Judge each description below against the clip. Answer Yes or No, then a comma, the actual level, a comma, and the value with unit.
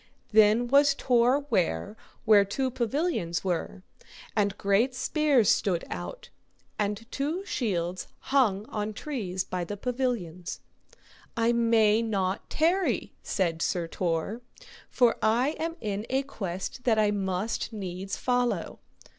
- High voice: Yes, high, 220 Hz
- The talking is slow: Yes, slow, 125 wpm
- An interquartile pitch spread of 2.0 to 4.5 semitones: No, average, 5.0 semitones